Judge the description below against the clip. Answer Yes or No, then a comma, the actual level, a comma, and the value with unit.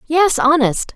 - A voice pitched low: No, very high, 290 Hz